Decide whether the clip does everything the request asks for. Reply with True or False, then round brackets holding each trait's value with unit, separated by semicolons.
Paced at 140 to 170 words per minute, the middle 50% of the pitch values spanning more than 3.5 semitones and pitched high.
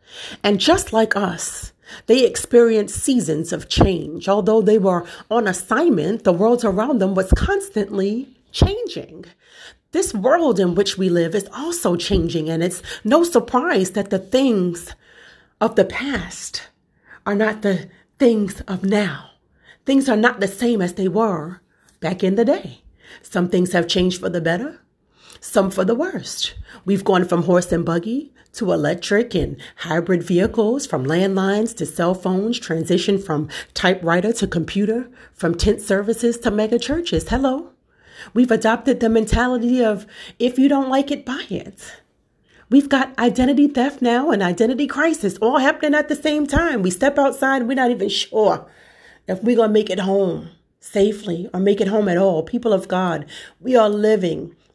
True (165 wpm; 5.0 semitones; 210 Hz)